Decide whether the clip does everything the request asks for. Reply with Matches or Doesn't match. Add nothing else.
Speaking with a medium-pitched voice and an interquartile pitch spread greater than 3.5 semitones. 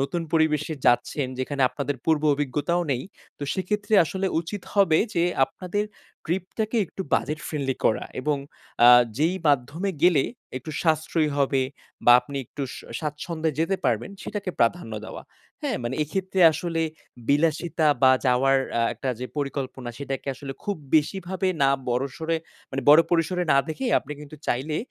Matches